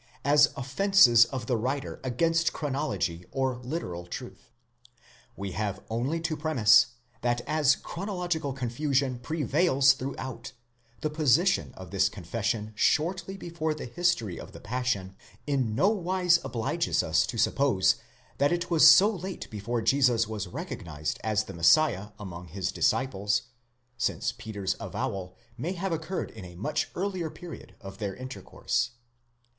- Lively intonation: Yes, wide, 6.8 semitones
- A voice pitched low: Yes, low, 130 Hz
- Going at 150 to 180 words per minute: No, average, 140 wpm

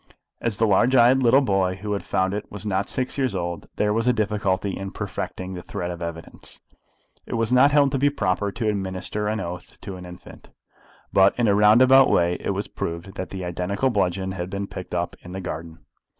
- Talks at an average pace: No, fast, 220 wpm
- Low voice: Yes, low, 100 Hz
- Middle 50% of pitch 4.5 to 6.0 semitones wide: No, average, 3.7 semitones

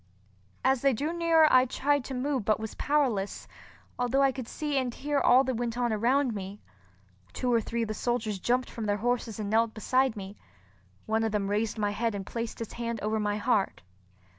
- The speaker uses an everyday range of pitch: Yes, average, 3.4 semitones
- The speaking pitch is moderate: No, high, 235 Hz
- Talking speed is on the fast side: Yes, fast, 210 wpm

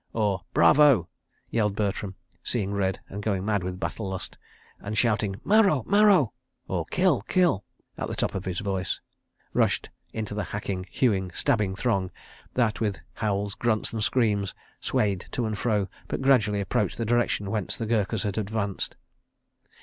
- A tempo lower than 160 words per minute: Yes, average, 150 wpm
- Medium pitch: No, low, 105 Hz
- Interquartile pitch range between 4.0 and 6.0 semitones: No, average, 2.8 semitones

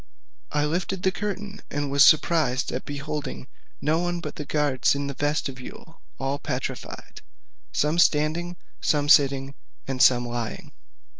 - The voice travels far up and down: No, average, 3.2 semitones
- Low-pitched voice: No, medium, 145 Hz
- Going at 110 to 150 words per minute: Yes, average, 145 wpm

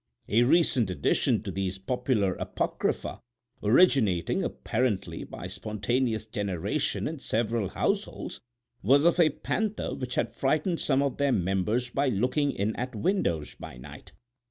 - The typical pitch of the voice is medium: No, low, 120 Hz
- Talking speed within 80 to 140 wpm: Yes, slow, 135 wpm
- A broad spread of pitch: Yes, wide, 5.8 semitones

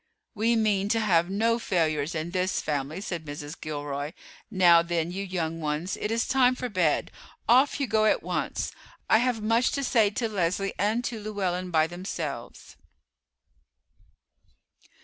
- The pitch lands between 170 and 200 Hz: Yes, medium, 185 Hz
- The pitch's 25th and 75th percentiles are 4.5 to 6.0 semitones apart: Yes, average, 5.2 semitones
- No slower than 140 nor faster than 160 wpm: Yes, average, 155 wpm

